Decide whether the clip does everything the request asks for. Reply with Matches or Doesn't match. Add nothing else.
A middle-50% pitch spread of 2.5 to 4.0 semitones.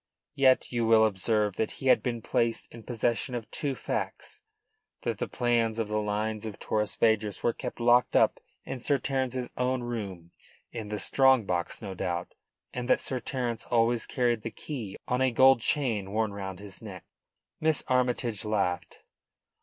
Matches